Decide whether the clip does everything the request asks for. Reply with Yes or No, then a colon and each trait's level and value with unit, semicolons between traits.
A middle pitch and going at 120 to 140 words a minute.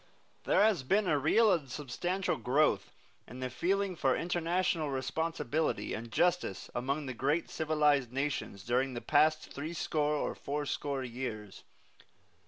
Yes: medium, 145 Hz; slow, 135 wpm